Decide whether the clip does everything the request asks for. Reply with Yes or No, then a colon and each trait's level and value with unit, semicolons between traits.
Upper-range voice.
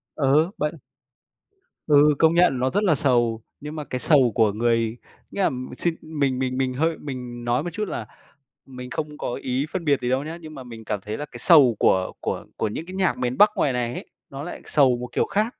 No: low, 135 Hz